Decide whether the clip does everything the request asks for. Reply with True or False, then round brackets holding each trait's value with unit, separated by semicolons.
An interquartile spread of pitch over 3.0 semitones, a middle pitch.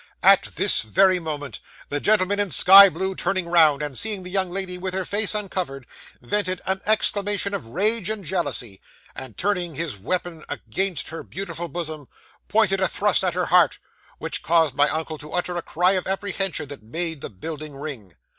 True (4.1 semitones; 180 Hz)